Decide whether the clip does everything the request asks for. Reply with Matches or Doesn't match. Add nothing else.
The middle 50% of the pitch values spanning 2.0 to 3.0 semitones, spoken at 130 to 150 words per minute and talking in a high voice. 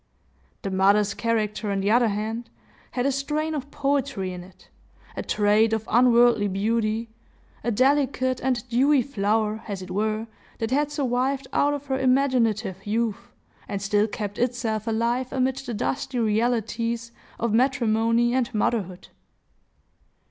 Doesn't match